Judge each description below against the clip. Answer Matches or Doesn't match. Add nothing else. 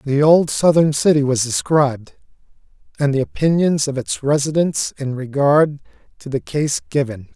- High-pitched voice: Doesn't match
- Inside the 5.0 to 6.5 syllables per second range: Doesn't match